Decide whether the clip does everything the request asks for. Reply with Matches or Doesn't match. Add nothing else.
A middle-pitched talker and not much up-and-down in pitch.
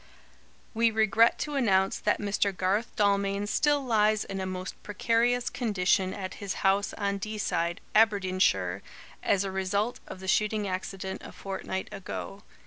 Doesn't match